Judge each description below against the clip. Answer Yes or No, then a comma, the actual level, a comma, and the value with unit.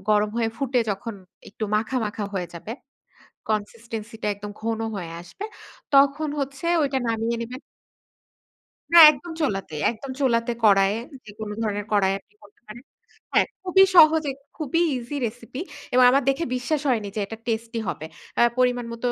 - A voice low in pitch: No, high, 230 Hz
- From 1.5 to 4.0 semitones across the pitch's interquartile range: No, average, 4.4 semitones